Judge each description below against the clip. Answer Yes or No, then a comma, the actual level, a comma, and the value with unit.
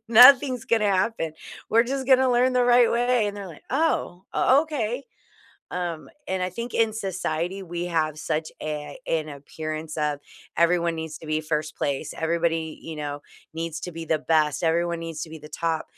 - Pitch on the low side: No, medium, 170 Hz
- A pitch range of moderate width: No, wide, 6.5 semitones